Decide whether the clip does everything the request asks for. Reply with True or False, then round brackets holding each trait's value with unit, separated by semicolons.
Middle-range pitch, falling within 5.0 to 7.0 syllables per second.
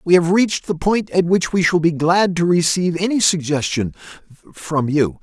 True (170 Hz; 5.1 syllables/s)